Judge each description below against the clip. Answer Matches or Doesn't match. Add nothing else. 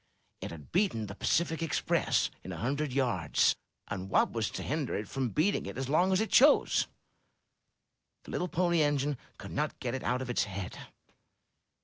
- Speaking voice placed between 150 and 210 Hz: Doesn't match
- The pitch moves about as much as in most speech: Doesn't match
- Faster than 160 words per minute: Matches